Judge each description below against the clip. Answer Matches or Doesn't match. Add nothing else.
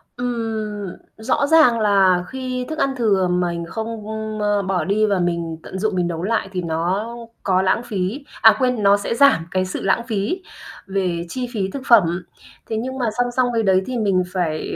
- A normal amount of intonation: Matches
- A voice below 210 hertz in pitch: Matches